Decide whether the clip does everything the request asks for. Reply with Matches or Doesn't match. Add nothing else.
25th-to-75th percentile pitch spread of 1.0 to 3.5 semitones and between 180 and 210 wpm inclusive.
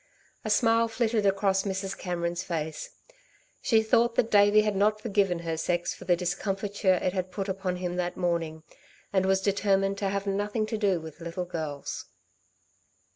Doesn't match